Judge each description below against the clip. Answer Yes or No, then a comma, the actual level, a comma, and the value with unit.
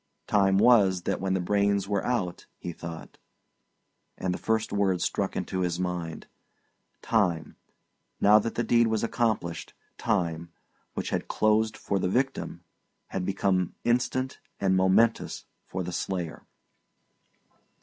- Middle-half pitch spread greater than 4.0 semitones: No, average, 3.6 semitones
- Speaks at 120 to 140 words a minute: Yes, slow, 135 wpm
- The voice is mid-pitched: No, very low, 95 Hz